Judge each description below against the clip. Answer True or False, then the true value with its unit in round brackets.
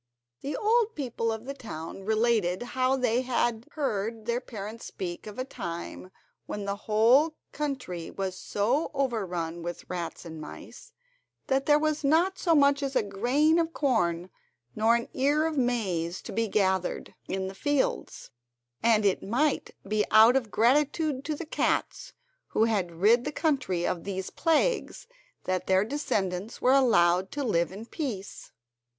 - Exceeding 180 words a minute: False (160 wpm)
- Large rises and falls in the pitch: True (6.4 semitones)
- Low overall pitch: False (230 Hz)